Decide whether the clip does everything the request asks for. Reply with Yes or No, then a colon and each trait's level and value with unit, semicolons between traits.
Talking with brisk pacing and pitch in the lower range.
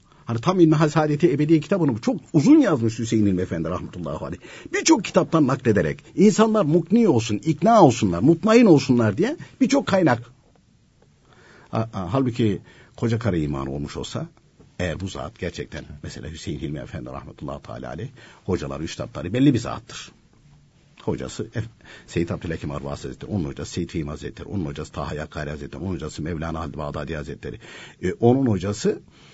Yes: fast, 150 wpm; low, 115 Hz